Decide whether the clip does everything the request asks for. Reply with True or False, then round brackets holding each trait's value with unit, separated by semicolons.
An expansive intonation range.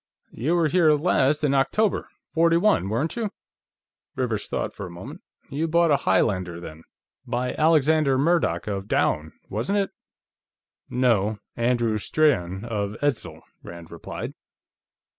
True (7.9 semitones)